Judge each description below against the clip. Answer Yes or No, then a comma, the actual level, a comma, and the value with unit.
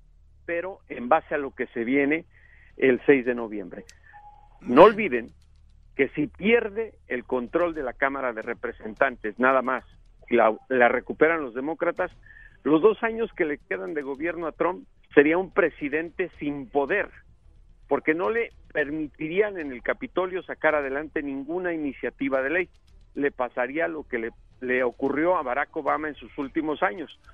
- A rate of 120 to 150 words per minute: No, average, 160 wpm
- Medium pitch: Yes, medium, 145 Hz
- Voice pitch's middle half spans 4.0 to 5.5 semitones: Yes, average, 5.1 semitones